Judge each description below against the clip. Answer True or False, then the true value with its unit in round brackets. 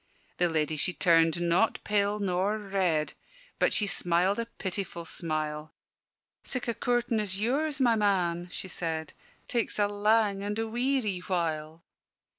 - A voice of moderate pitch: False (195 Hz)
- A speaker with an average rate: True (145 wpm)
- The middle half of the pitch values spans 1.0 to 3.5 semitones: False (4.3 semitones)